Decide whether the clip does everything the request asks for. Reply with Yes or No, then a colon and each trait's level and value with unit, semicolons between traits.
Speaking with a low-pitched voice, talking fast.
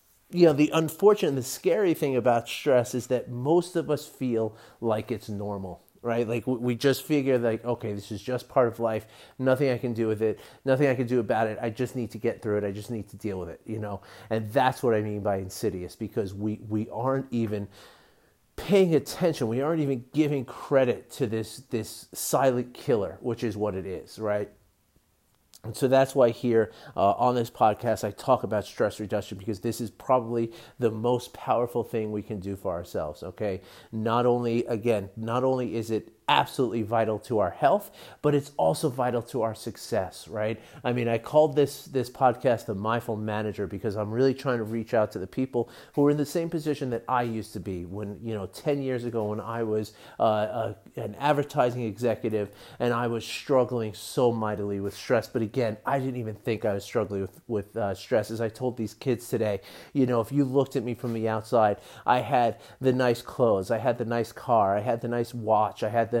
Yes: low, 115 Hz; fast, 215 wpm